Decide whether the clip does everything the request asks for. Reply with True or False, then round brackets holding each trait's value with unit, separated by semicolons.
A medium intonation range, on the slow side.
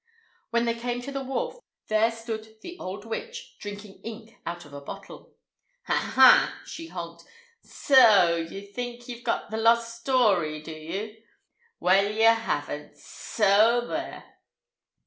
False (3.4 semitones; 155 wpm)